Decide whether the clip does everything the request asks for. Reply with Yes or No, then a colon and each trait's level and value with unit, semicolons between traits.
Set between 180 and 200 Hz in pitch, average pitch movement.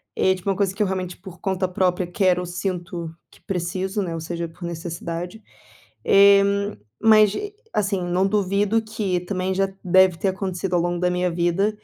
No: medium, 185 Hz; narrow, 1.9 semitones